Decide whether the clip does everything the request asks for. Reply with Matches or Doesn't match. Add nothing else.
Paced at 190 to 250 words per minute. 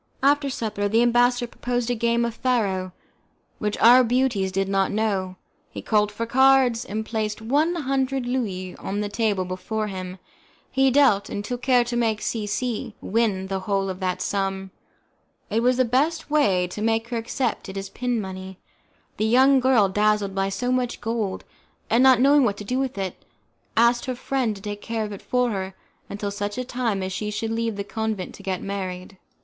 Matches